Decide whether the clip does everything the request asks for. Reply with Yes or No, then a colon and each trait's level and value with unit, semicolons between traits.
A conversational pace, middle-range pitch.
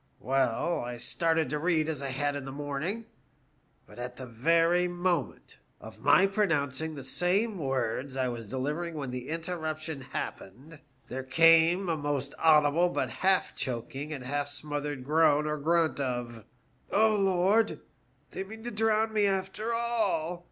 Yes: average, 160 wpm; medium, 155 Hz